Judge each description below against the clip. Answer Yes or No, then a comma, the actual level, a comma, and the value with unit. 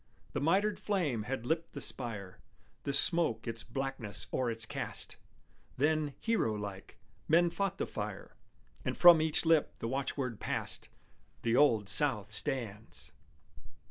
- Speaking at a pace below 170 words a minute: Yes, average, 140 wpm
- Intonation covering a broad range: Yes, wide, 6.2 semitones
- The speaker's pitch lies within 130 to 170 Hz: Yes, low, 135 Hz